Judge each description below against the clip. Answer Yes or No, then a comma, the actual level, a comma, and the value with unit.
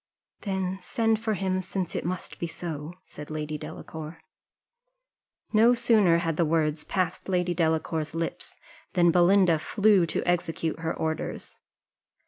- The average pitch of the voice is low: No, medium, 175 Hz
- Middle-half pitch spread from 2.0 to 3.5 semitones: Yes, average, 3.0 semitones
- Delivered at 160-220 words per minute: No, slow, 135 wpm